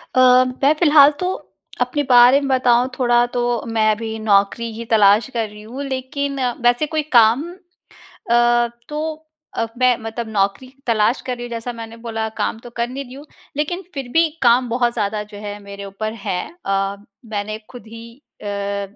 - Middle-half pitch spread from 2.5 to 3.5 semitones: Yes, average, 3.0 semitones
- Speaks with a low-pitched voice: No, high, 235 Hz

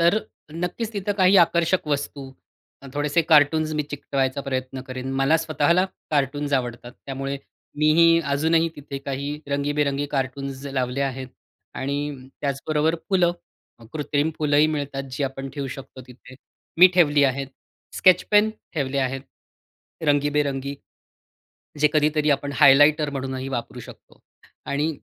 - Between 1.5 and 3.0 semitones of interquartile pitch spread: Yes, narrow, 2.4 semitones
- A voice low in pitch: No, medium, 145 Hz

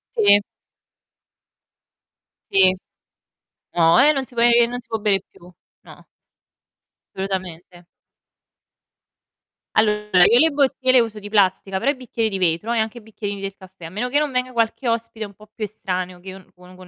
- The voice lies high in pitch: Yes, high, 210 Hz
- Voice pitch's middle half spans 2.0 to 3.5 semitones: No, average, 3.9 semitones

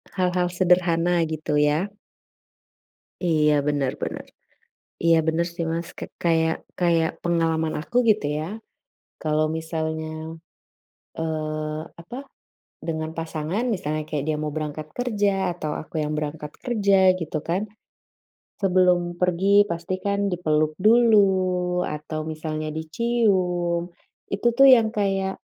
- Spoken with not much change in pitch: No, average, 3.1 semitones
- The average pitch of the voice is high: No, medium, 170 Hz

